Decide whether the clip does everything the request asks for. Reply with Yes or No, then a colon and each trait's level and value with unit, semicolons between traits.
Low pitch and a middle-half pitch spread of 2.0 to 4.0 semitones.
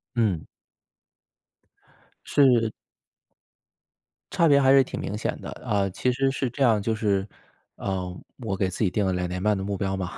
No: low, 105 Hz; average, 4.6 semitones